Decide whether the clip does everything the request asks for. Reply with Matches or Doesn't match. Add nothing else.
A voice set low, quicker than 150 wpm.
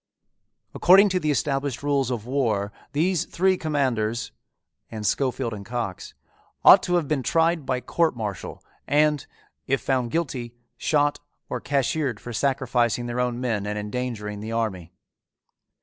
Doesn't match